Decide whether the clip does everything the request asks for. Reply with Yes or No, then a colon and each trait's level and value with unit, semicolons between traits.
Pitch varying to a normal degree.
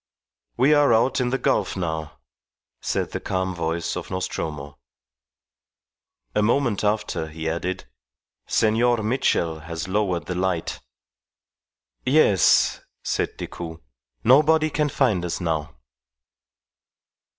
No: wide, 6.9 semitones